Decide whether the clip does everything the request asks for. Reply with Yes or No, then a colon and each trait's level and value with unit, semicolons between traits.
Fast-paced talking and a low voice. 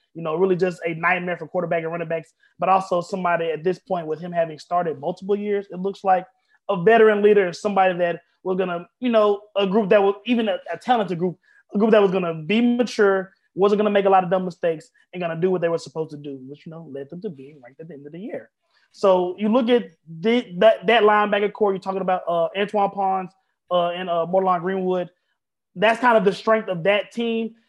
No: fast, 240 wpm; high, 190 Hz